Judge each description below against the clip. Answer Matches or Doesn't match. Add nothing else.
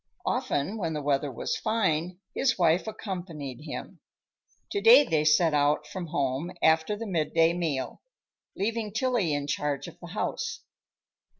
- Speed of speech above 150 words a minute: Doesn't match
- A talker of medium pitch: Matches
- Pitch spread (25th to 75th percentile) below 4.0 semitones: Doesn't match